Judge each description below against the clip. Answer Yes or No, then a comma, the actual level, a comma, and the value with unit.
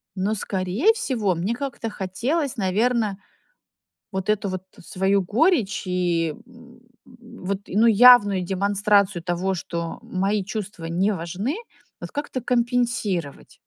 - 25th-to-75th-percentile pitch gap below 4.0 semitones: No, average, 4.4 semitones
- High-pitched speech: Yes, high, 200 Hz